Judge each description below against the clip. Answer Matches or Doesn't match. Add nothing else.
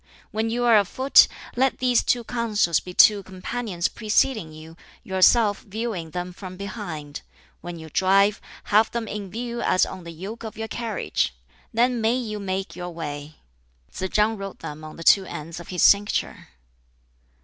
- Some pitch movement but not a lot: Matches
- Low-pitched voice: Doesn't match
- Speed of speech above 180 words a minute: Doesn't match